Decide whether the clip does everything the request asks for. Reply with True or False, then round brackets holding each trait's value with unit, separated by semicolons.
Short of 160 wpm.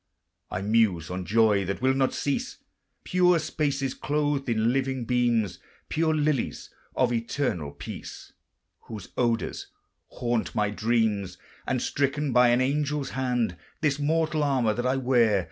True (140 wpm)